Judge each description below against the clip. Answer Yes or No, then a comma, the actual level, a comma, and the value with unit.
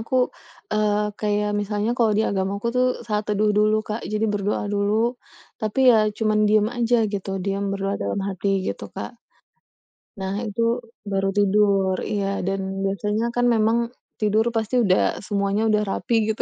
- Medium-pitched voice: No, high, 210 Hz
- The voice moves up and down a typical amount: No, narrow, 1.4 semitones